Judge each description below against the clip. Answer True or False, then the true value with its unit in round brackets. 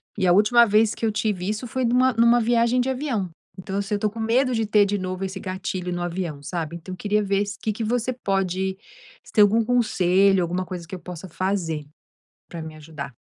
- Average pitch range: True (3.8 semitones)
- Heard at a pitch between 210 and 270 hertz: False (200 Hz)